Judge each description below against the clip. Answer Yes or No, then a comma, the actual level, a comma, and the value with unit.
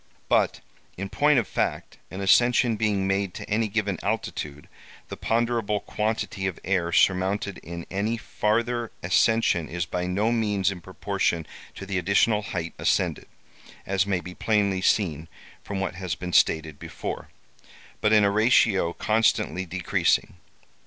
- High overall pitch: No, low, 100 Hz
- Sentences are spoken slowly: No, average, 145 wpm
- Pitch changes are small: No, average, 3.0 semitones